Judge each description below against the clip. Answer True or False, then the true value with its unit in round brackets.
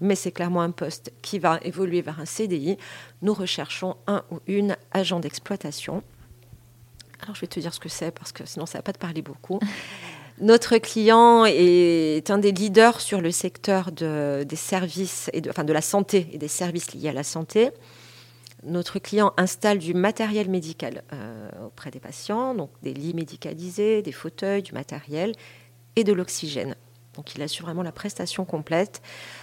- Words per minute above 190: False (180 wpm)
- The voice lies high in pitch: False (175 Hz)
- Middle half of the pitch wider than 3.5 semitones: True (4.6 semitones)